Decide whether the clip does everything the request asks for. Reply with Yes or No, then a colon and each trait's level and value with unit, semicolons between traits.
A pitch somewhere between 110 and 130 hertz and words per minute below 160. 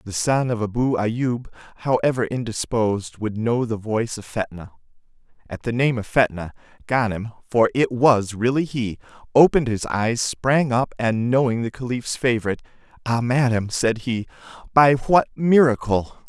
Yes: low, 120 Hz; average, 150 wpm